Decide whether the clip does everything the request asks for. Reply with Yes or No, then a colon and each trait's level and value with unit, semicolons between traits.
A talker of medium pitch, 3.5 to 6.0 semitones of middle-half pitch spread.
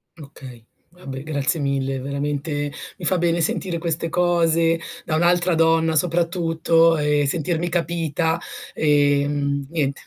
No: medium, 160 Hz; average, 2.7 semitones